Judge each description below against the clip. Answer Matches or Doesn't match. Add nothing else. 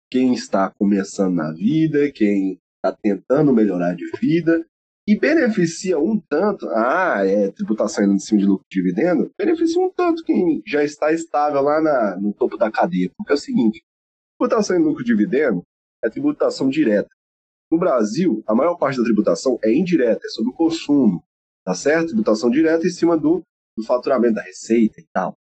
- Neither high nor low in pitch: Matches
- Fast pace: Doesn't match